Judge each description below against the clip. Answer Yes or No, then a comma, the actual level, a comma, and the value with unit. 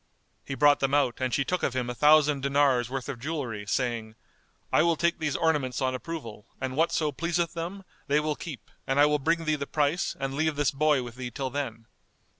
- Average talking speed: No, fast, 220 wpm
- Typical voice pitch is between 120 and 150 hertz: Yes, medium, 140 Hz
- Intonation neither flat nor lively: Yes, average, 3.2 semitones